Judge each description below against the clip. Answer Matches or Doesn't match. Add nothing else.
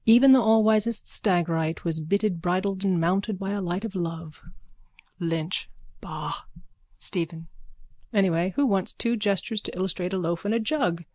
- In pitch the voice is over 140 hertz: Matches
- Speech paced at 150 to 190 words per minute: Matches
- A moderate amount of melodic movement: Matches